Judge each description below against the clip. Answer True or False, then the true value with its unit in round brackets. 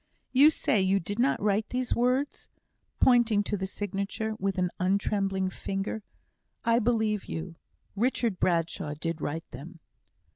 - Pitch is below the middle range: False (200 Hz)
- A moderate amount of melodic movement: True (3.9 semitones)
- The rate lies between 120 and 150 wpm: True (140 wpm)